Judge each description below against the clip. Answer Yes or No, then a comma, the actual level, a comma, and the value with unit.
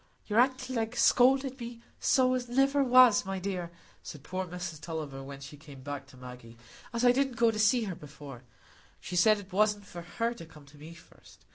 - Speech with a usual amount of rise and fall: No, wide, 8.3 semitones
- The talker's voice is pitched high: Yes, high, 195 Hz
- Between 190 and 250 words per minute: Yes, fast, 205 wpm